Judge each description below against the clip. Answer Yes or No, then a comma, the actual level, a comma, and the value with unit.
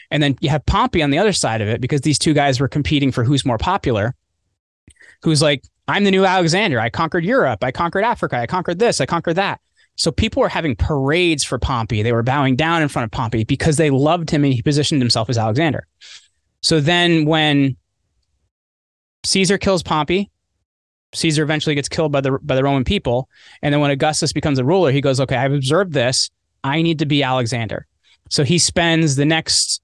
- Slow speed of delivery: No, fast, 205 wpm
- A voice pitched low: No, medium, 145 Hz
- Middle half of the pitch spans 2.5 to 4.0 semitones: No, average, 4.7 semitones